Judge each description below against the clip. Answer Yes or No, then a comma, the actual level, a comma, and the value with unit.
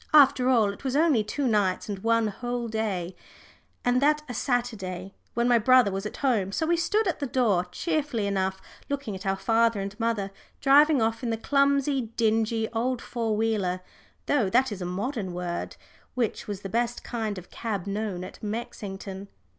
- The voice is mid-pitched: No, high, 225 Hz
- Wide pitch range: No, average, 4.2 semitones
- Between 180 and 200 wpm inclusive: Yes, average, 185 wpm